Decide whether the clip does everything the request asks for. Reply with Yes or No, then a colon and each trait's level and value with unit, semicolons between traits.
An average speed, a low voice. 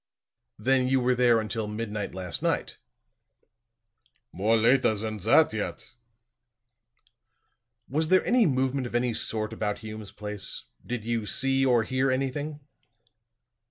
No: slow, 125 wpm; low, 120 Hz